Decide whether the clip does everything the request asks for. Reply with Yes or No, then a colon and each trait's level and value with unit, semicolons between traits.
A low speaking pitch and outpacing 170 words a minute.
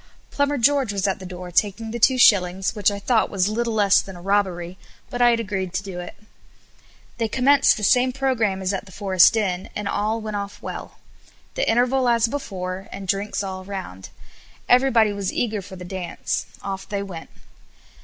No: high, 200 Hz; average, 195 wpm